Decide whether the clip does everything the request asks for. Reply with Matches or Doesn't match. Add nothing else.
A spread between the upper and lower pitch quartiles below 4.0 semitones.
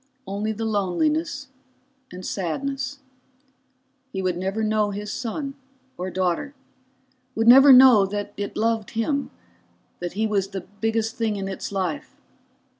Doesn't match